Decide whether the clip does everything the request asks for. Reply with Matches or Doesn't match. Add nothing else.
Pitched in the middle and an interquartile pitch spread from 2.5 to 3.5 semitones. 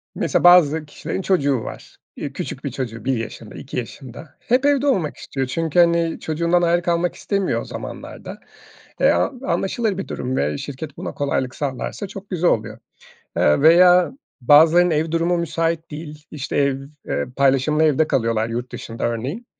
Doesn't match